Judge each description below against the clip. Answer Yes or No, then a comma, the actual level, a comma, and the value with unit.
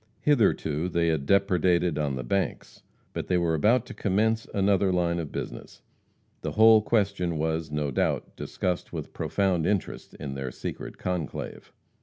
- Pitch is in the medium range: No, very low, 90 Hz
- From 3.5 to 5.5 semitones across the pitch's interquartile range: Yes, average, 4.0 semitones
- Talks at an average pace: Yes, average, 155 wpm